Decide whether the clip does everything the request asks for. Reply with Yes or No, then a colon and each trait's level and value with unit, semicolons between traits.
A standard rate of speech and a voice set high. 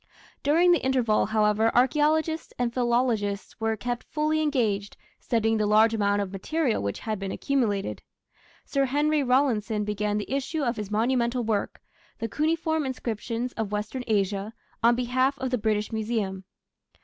Yes: average, 150 wpm; high, 230 Hz